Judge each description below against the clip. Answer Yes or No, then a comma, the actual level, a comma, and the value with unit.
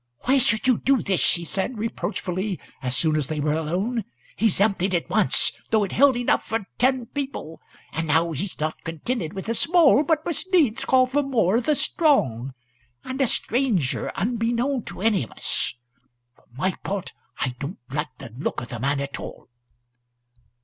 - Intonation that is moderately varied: No, wide, 8.2 semitones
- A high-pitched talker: Yes, high, 205 Hz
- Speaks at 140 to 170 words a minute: No, average, 185 wpm